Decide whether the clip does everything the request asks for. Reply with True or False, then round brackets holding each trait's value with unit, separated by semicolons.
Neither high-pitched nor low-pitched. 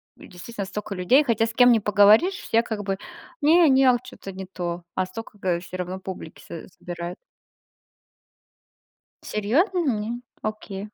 False (210 Hz)